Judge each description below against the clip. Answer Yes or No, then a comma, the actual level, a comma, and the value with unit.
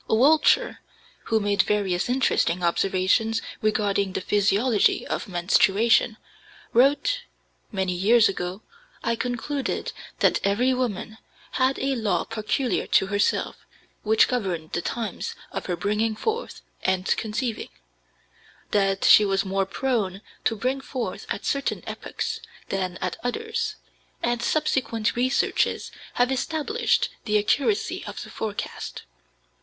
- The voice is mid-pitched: No, high, 220 Hz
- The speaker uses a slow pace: Yes, slow, 120 wpm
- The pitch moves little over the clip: No, average, 4.5 semitones